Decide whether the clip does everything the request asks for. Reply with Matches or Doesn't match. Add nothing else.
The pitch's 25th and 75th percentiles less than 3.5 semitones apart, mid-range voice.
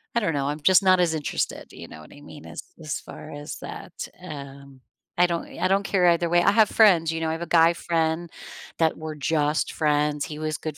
Matches